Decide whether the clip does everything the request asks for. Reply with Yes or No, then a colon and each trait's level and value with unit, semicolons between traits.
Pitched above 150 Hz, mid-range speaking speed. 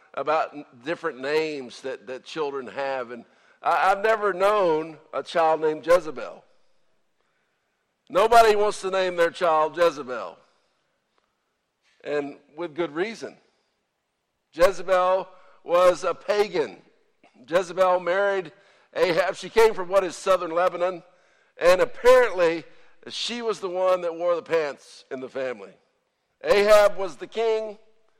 No: medium, 185 Hz; slow, 125 wpm